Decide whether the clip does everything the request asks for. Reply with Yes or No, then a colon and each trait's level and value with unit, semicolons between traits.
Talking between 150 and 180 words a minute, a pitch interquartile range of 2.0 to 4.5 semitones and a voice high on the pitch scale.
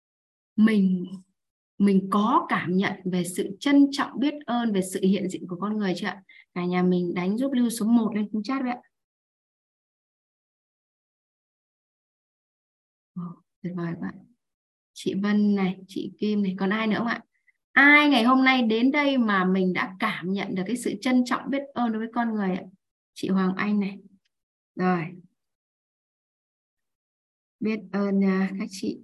Yes: slow, 165 wpm; average, 4.1 semitones; high, 205 Hz